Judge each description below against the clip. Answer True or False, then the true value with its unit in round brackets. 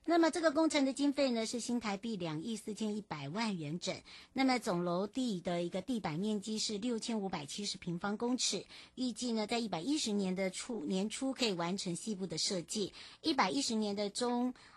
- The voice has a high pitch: True (215 Hz)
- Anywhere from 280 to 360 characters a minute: True (305 characters per minute)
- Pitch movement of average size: True (4.3 semitones)